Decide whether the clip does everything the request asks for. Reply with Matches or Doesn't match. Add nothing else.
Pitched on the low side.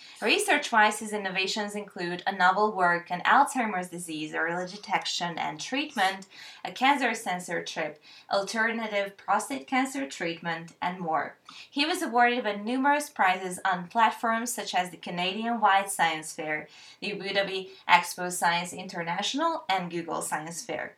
Doesn't match